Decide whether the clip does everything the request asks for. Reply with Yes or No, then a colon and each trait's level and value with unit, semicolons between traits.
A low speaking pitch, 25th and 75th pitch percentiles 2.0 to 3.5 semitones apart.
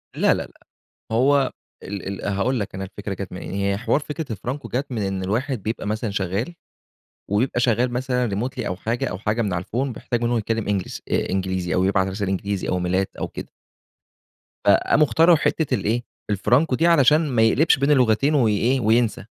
No: low, 110 Hz; average, 4.7 semitones